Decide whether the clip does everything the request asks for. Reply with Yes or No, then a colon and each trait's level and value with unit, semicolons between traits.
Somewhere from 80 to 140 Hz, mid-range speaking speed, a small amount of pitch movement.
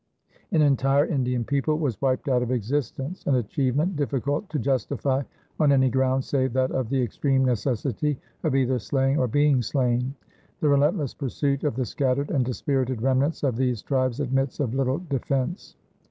Yes: low, 135 Hz; average, 170 wpm; narrow, 2.0 semitones